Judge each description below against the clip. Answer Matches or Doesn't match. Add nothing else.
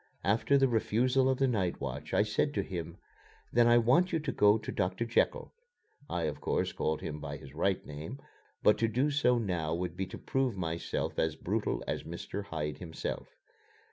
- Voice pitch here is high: Doesn't match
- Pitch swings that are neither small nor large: Doesn't match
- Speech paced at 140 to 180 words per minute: Doesn't match